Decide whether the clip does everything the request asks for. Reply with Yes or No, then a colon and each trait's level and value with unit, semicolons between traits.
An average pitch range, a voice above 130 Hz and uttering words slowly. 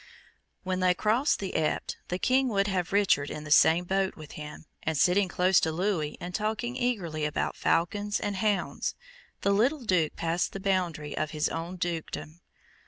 No: average, 3.9 semitones; medium, 185 Hz; average, 175 wpm